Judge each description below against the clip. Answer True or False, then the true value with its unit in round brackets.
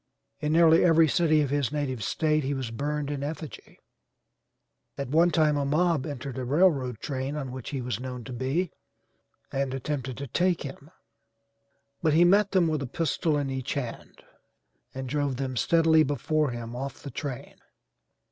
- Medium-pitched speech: True (145 Hz)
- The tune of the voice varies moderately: True (3.2 semitones)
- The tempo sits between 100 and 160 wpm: False (175 wpm)